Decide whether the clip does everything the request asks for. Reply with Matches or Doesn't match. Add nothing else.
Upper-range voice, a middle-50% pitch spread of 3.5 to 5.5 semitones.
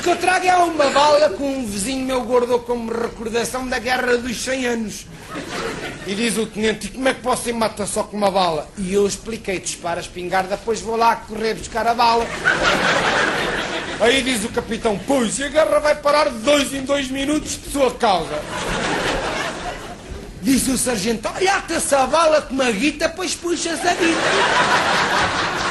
Matches